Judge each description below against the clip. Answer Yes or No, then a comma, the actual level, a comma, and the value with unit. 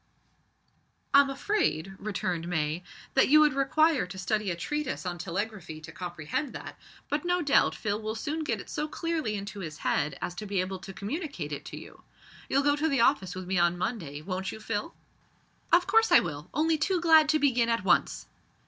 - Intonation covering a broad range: Yes, wide, 8.8 semitones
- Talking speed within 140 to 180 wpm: No, average, 200 wpm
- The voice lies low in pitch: No, high, 215 Hz